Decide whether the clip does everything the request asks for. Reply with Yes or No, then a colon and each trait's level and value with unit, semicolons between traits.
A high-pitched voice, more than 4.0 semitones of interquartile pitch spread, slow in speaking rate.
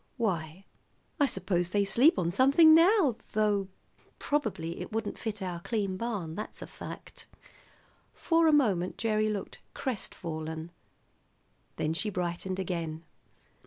Yes: high, 200 Hz; average, 5.1 semitones; slow, 125 wpm